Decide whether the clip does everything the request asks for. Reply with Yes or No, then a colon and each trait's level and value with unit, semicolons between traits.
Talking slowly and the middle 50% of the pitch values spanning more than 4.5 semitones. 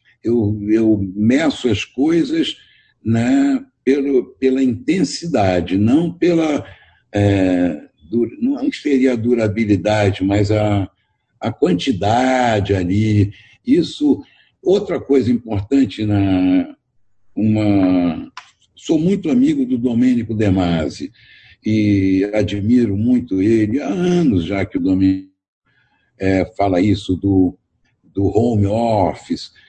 Yes: slow, 105 wpm; average, 5.1 semitones